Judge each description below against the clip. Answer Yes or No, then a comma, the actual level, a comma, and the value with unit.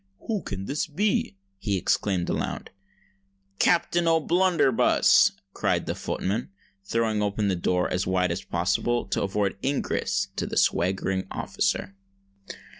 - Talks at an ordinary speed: No, slow, 125 wpm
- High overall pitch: No, low, 100 Hz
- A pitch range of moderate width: No, wide, 6.9 semitones